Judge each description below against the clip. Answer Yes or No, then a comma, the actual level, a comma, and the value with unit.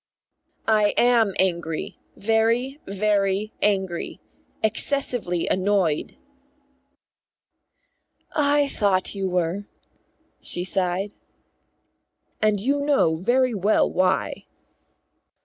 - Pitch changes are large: No, average, 3.8 semitones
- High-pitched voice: Yes, high, 205 Hz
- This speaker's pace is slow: Yes, slow, 80 wpm